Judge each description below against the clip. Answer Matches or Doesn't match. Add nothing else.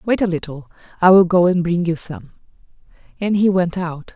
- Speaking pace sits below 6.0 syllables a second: Matches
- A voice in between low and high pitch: Matches